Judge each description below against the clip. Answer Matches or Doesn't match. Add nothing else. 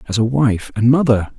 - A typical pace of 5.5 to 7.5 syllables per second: Doesn't match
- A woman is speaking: Doesn't match